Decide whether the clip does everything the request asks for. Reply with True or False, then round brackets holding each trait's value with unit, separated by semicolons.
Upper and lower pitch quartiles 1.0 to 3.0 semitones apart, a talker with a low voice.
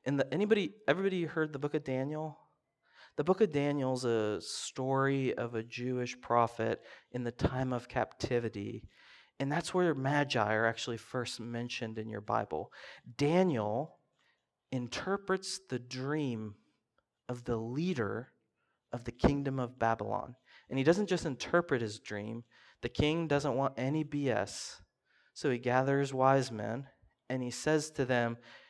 False (3.7 semitones; 130 Hz)